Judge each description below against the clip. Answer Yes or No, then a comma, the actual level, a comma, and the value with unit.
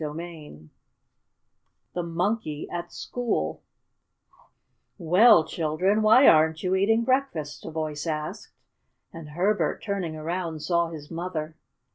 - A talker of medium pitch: Yes, medium, 170 Hz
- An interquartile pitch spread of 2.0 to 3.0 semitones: No, average, 3.9 semitones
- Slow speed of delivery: Yes, slow, 115 wpm